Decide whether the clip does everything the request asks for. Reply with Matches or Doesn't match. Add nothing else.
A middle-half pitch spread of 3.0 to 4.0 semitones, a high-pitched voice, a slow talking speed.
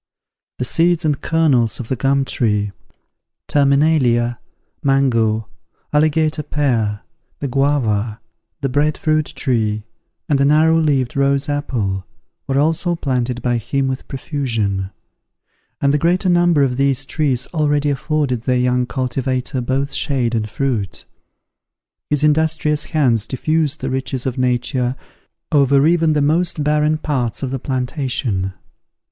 Doesn't match